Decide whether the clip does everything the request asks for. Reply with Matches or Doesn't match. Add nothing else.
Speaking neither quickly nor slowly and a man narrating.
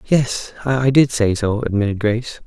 Matches